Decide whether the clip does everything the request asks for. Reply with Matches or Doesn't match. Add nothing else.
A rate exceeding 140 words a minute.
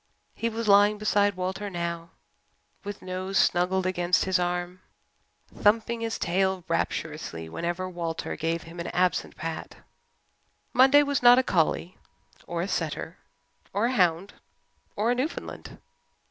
Doesn't match